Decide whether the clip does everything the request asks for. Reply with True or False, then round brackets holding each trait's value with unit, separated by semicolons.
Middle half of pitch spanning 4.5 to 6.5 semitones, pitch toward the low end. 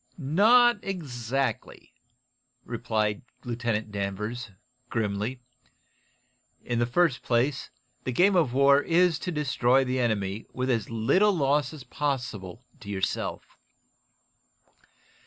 True (4.8 semitones; 125 Hz)